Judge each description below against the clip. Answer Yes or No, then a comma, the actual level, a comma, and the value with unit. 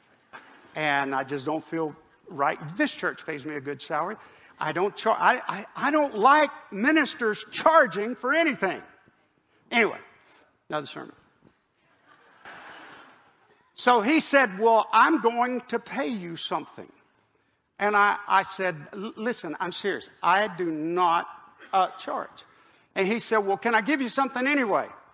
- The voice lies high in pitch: Yes, high, 215 Hz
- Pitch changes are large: Yes, wide, 7.1 semitones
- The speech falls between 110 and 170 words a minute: Yes, average, 145 wpm